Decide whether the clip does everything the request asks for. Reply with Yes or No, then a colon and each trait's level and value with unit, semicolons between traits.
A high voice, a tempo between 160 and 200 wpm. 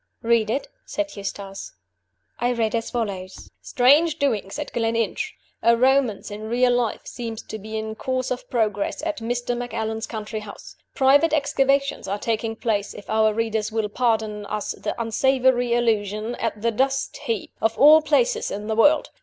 Yes: high, 230 Hz; average, 165 wpm